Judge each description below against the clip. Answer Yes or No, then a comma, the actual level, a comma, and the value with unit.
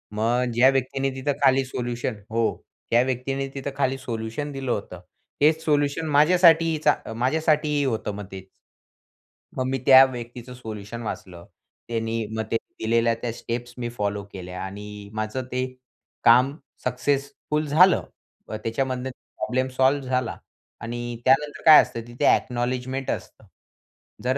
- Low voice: Yes, low, 125 Hz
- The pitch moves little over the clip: No, average, 3.1 semitones